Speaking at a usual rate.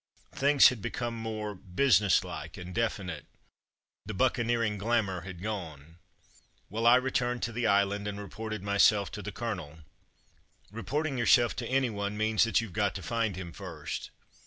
Yes: average, 155 wpm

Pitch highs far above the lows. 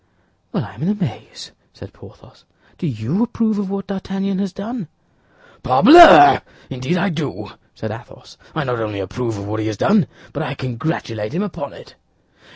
Yes: wide, 8.6 semitones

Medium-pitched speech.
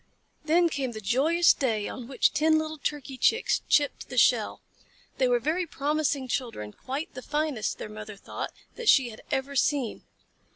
No: very high, 275 Hz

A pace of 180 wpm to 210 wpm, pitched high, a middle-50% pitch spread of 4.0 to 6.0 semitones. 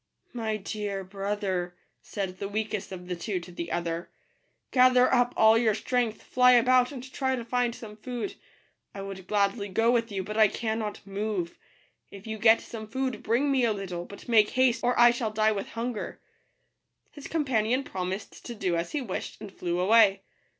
No: average, 190 wpm; high, 215 Hz; average, 3.6 semitones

